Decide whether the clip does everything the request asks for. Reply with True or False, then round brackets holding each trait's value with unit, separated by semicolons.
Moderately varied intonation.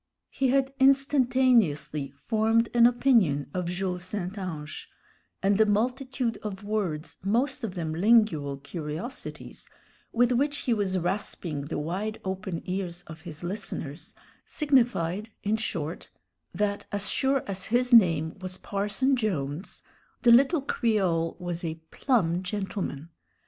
False (5.9 semitones)